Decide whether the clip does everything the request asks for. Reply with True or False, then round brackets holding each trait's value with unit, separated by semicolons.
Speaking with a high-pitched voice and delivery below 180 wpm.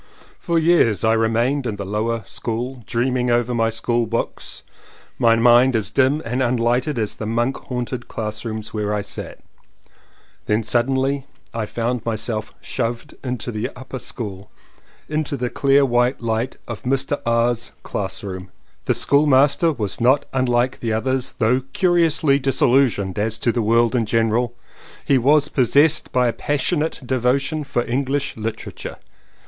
False (120 Hz; 150 wpm)